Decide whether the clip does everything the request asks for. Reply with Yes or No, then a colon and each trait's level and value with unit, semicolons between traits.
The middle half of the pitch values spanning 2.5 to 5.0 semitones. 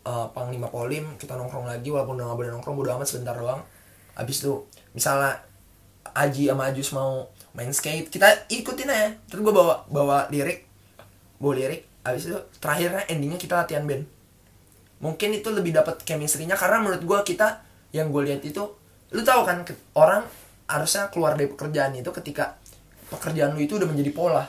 No: wide, 5.6 semitones